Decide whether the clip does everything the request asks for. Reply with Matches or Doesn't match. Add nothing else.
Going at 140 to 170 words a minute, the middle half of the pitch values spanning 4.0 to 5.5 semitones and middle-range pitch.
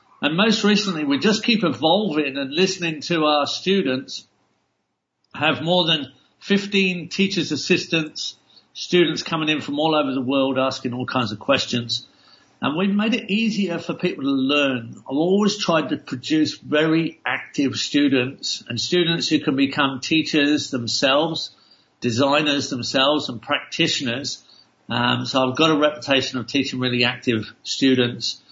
Matches